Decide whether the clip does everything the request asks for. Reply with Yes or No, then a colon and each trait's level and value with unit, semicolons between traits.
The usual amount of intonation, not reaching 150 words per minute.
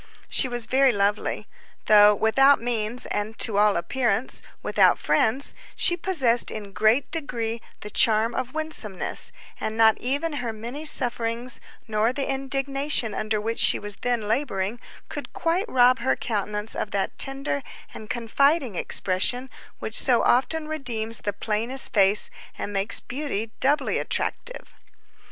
Yes: average, 4.1 semitones; average, 140 wpm